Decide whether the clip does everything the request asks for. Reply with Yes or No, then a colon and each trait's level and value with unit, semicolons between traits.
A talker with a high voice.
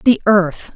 Yes: high, 200 Hz